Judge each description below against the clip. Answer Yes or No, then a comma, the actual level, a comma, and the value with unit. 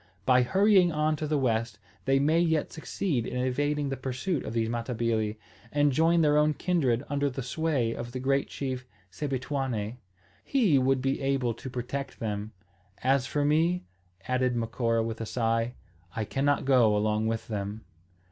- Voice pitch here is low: Yes, low, 130 Hz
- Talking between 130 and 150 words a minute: No, average, 165 wpm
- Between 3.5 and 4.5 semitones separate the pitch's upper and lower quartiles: Yes, average, 4.1 semitones